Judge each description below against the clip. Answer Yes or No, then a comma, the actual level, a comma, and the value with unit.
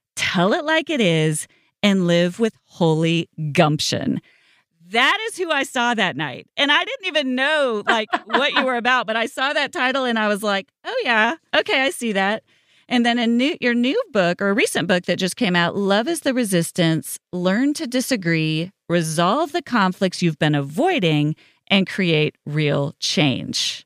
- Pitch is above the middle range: Yes, high, 205 Hz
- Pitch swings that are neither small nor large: No, wide, 7.0 semitones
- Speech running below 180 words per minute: No, average, 185 wpm